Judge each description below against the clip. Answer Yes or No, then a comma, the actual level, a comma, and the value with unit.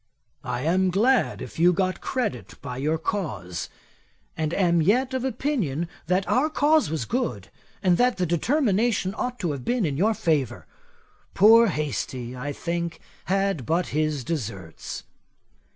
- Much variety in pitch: Yes, wide, 7.4 semitones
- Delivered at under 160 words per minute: Yes, average, 150 wpm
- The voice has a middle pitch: Yes, medium, 175 Hz